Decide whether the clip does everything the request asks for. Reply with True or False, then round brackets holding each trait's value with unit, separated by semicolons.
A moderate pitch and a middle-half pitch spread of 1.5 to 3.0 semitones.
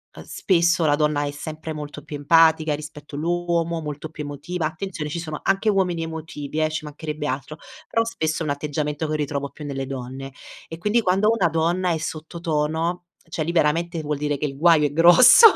True (155 Hz; 2.4 semitones)